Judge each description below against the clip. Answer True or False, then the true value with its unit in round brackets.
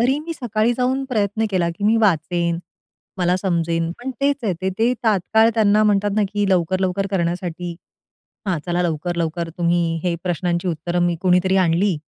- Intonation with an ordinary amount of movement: True (3.6 semitones)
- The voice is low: False (185 Hz)